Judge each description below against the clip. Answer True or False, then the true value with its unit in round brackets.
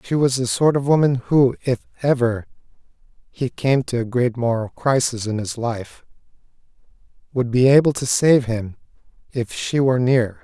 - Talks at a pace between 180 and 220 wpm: False (165 wpm)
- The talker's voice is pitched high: False (125 Hz)